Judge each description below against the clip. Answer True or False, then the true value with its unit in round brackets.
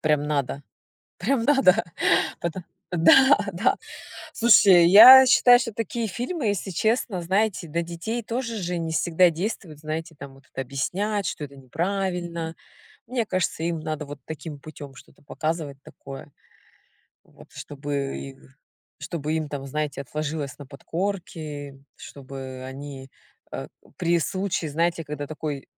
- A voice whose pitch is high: False (165 Hz)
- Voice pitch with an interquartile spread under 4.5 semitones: False (5.2 semitones)